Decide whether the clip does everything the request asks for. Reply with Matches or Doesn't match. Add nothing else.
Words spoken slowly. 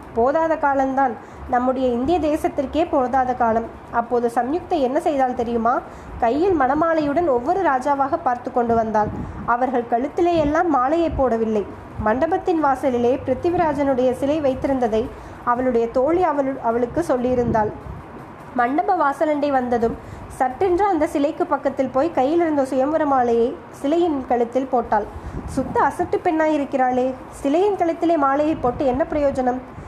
Doesn't match